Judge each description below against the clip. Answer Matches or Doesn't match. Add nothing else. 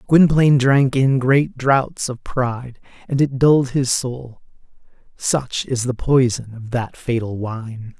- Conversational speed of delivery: Matches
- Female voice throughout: Doesn't match